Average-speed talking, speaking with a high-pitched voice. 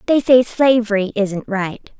Yes: average, 150 wpm; high, 220 Hz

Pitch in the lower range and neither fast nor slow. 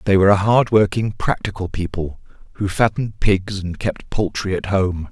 Yes: very low, 95 Hz; average, 165 wpm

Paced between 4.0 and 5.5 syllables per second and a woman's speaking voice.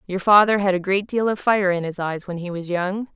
Yes: 5.4 syllables/s; female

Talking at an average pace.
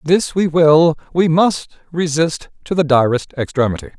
Yes: average, 150 wpm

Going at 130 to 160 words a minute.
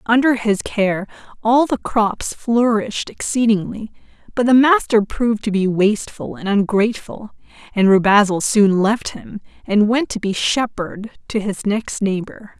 Yes: average, 150 wpm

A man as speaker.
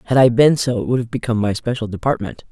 No: female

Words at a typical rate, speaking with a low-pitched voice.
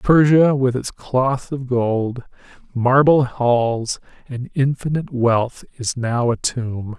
No: slow, 130 wpm; low, 125 Hz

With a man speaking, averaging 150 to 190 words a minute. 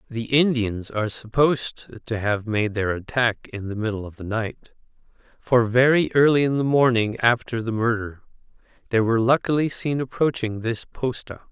Yes: male; average, 160 wpm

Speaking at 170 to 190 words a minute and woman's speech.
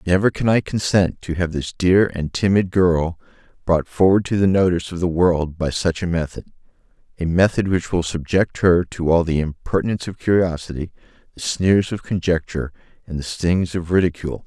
No: average, 185 wpm; male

